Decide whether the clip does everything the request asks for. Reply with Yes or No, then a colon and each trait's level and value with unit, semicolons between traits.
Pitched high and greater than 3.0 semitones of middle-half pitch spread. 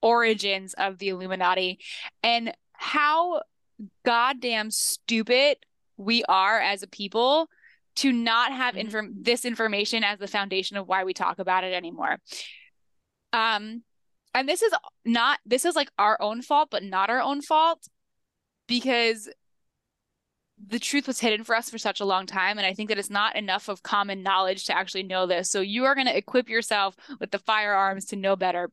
Yes: high, 215 Hz; average, 3.9 semitones